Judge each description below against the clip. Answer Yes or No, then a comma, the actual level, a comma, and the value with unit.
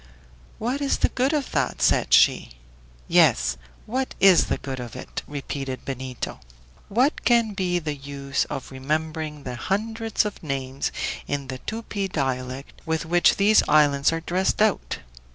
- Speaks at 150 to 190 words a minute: Yes, average, 155 wpm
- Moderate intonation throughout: No, wide, 7.3 semitones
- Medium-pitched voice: Yes, medium, 155 Hz